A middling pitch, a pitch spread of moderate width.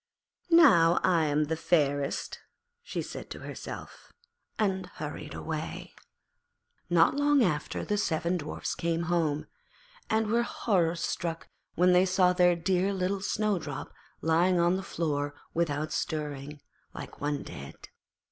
Yes: medium, 170 Hz; average, 3.6 semitones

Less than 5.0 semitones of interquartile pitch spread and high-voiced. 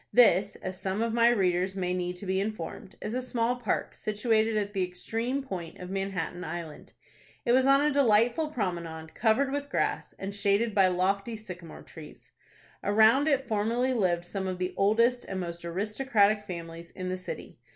Yes: average, 4.3 semitones; high, 200 Hz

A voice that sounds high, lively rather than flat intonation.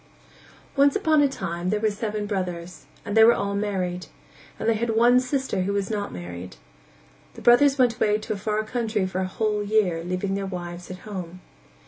No: high, 205 Hz; average, 3.5 semitones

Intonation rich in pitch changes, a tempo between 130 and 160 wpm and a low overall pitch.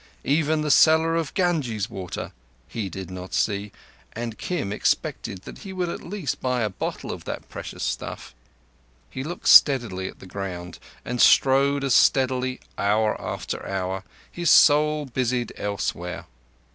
Yes: wide, 7.3 semitones; average, 150 wpm; low, 125 Hz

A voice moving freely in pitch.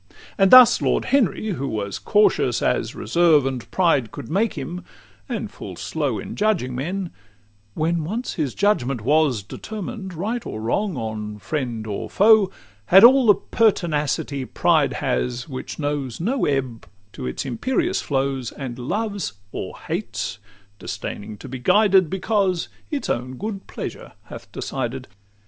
Yes: wide, 8.1 semitones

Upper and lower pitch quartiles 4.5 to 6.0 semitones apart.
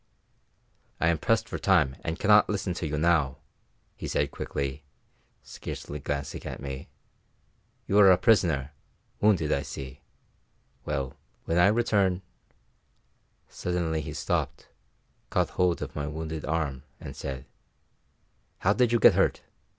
Yes: average, 5.2 semitones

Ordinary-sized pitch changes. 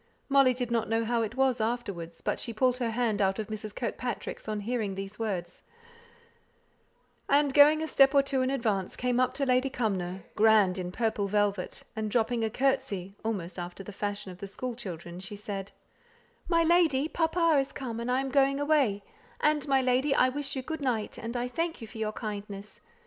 Yes: average, 4.7 semitones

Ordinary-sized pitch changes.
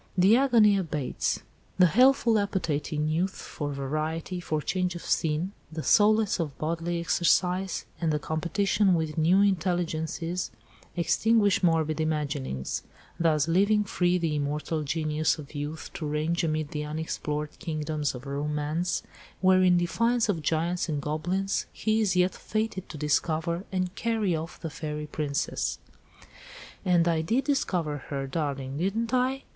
Yes: average, 3.7 semitones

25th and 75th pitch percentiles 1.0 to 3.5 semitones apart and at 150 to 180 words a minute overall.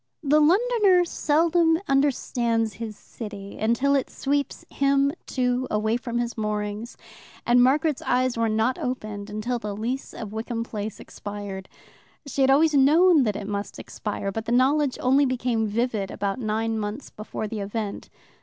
No: average, 4.5 semitones; average, 155 wpm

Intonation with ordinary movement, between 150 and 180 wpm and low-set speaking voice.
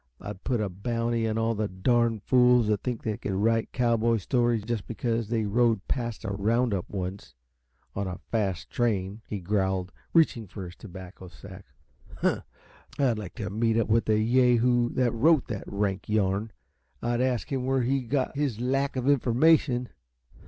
Yes: average, 3.2 semitones; average, 175 wpm; low, 115 Hz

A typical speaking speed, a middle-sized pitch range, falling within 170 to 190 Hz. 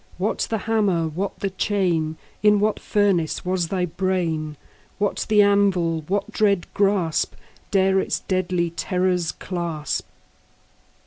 No: slow, 130 wpm; average, 3.0 semitones; medium, 185 Hz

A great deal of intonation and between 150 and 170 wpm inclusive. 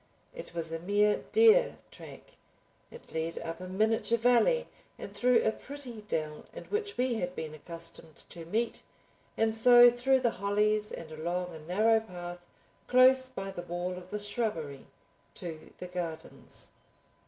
Yes: wide, 6.0 semitones; average, 155 wpm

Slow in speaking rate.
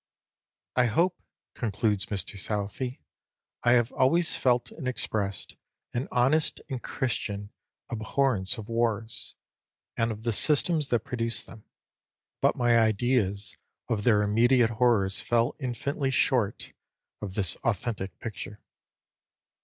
Yes: slow, 120 wpm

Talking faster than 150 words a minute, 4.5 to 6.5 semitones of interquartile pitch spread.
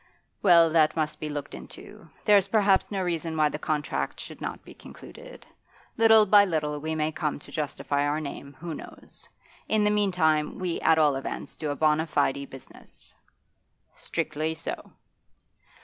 No: average, 165 wpm; average, 3.7 semitones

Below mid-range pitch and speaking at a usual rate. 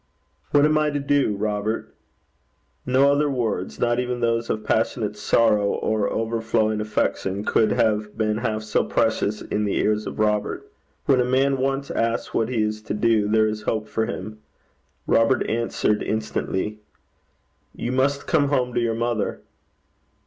Yes: low, 110 Hz; average, 160 wpm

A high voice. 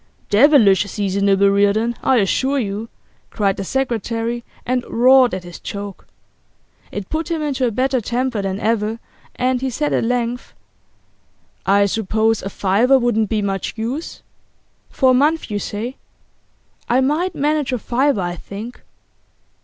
Yes: high, 230 Hz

